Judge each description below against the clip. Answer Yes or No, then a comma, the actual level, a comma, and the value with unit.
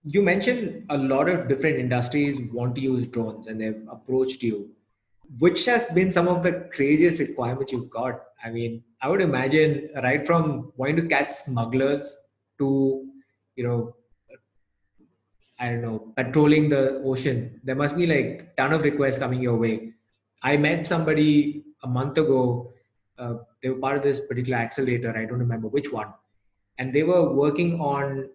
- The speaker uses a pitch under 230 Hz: Yes, low, 135 Hz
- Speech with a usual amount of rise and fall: Yes, average, 3.9 semitones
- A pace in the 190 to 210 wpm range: No, average, 165 wpm